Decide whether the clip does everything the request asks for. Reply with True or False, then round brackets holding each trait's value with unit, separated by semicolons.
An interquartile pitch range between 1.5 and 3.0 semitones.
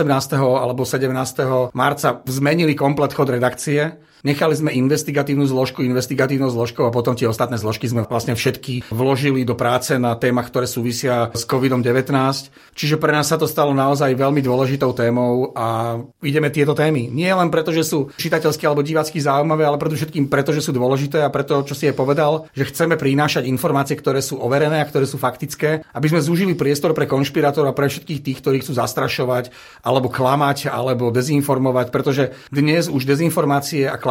True (2.7 semitones)